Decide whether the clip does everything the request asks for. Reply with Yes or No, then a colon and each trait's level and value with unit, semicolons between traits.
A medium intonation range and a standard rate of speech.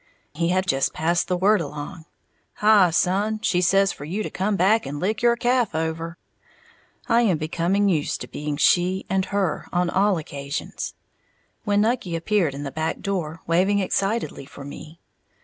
Yes: average, 4.1 semitones; average, 170 wpm